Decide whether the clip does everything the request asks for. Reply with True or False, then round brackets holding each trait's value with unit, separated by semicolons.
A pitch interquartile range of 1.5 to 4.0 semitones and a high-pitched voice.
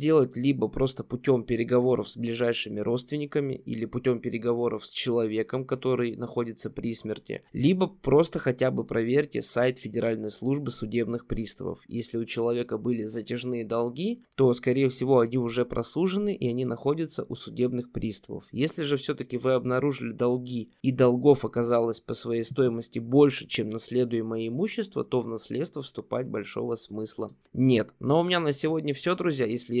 False (2.8 semitones; 125 Hz)